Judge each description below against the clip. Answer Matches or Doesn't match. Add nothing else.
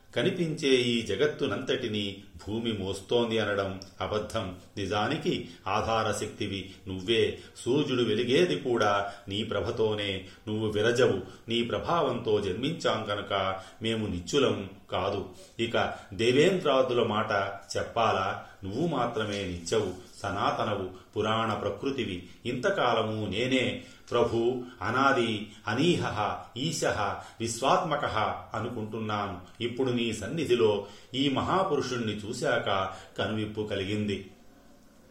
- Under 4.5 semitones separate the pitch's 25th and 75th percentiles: Matches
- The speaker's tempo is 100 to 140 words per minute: Doesn't match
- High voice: Doesn't match